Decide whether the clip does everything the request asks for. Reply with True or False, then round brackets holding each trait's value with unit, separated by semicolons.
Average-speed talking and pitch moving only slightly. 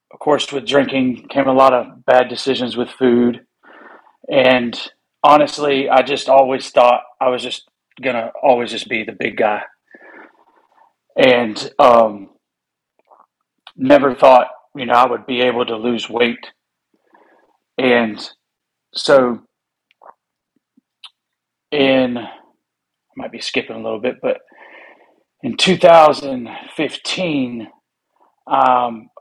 False (110 wpm; 2.0 semitones)